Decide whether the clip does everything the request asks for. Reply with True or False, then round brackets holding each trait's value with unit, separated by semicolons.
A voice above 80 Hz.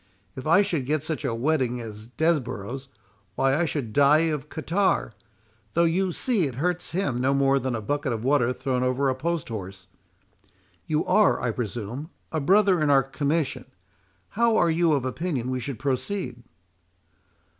True (140 Hz)